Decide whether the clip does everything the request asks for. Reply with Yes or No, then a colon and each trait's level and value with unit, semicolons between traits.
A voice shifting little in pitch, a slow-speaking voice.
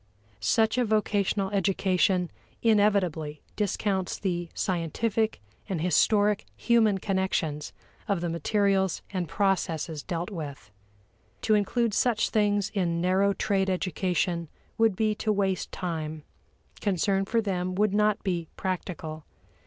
No: average, 3.2 semitones; slow, 120 wpm